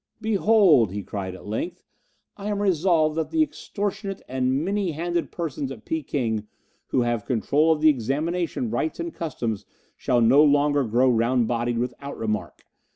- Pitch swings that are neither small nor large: No, wide, 6.2 semitones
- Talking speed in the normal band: Yes, average, 160 wpm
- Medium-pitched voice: Yes, medium, 145 Hz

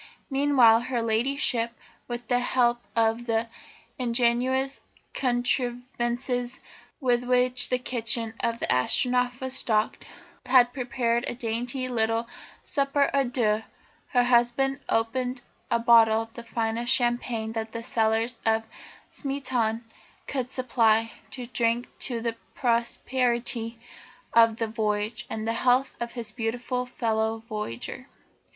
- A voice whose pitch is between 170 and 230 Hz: No, high, 240 Hz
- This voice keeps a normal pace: No, slow, 125 wpm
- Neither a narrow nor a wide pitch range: No, narrow, 1.8 semitones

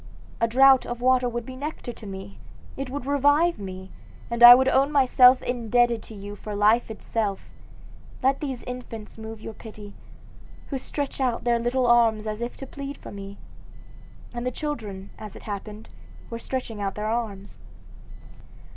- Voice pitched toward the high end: Yes, high, 235 Hz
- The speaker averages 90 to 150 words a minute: No, average, 170 wpm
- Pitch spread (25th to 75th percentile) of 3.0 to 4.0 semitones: Yes, average, 3.5 semitones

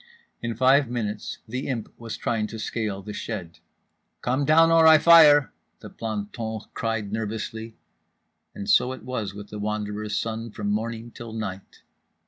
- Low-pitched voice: Yes, low, 115 Hz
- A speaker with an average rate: Yes, average, 155 wpm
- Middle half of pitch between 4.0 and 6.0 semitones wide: No, average, 2.9 semitones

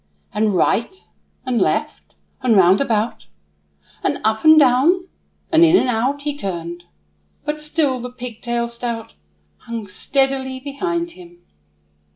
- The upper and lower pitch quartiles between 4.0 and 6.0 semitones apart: Yes, average, 4.7 semitones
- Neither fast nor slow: No, slow, 130 wpm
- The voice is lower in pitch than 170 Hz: No, very high, 250 Hz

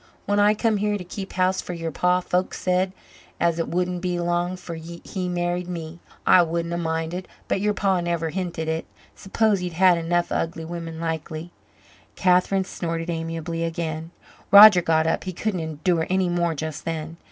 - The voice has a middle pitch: Yes, medium, 175 Hz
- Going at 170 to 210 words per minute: Yes, average, 185 wpm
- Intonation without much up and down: Yes, narrow, 1.9 semitones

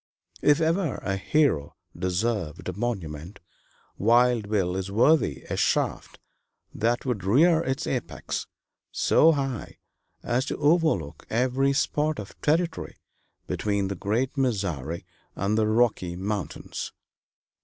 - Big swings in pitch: Yes, wide, 6.2 semitones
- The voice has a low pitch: Yes, low, 115 Hz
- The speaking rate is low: Yes, slow, 120 wpm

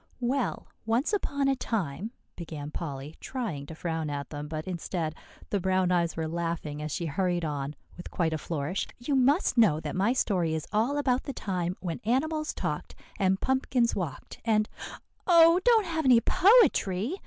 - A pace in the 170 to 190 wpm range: Yes, average, 175 wpm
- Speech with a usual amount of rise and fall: No, wide, 8.3 semitones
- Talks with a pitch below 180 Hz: No, medium, 185 Hz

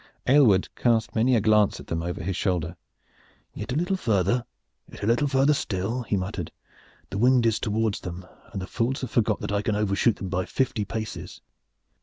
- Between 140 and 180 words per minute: No, average, 195 wpm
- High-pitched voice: No, low, 110 Hz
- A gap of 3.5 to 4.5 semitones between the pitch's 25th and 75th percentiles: Yes, average, 4.0 semitones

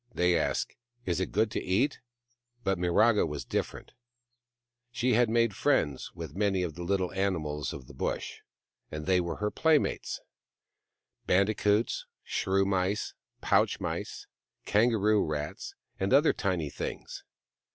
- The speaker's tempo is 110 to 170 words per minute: Yes, average, 140 wpm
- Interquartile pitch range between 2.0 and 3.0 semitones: No, average, 4.1 semitones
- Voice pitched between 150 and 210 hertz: No, very low, 95 Hz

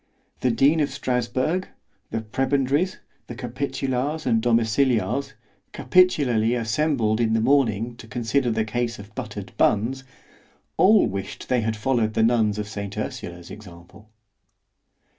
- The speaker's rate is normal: No, slow, 130 wpm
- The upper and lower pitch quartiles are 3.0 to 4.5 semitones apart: Yes, average, 3.6 semitones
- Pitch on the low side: Yes, low, 120 Hz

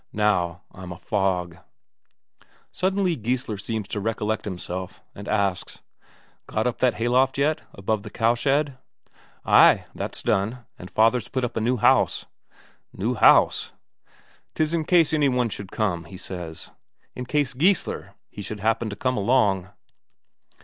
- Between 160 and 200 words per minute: No, average, 145 wpm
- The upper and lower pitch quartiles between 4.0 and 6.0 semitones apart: Yes, average, 4.6 semitones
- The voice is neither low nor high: No, low, 110 Hz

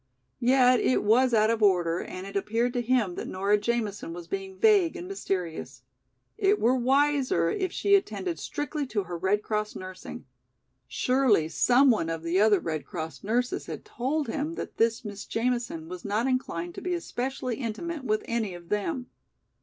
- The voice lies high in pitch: Yes, high, 230 Hz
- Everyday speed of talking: Yes, average, 175 wpm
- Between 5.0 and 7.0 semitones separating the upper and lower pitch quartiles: Yes, wide, 5.6 semitones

